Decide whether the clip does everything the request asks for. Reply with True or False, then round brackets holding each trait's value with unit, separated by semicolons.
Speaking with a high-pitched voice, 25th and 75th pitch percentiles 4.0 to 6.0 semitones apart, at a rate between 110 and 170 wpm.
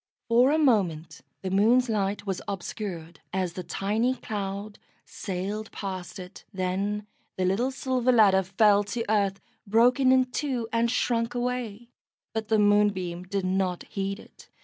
False (205 Hz; 3.5 semitones; 150 wpm)